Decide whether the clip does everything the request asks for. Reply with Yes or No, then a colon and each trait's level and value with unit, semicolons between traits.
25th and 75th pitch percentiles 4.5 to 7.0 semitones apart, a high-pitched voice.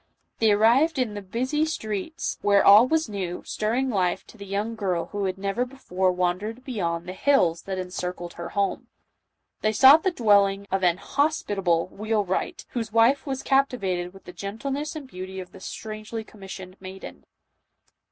Yes: average, 4.8 semitones; high, 205 Hz